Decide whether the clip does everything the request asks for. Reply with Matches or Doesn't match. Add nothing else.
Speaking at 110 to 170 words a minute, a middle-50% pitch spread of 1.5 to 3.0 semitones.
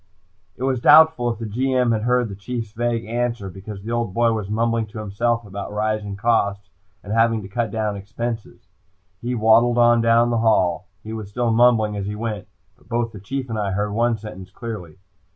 Doesn't match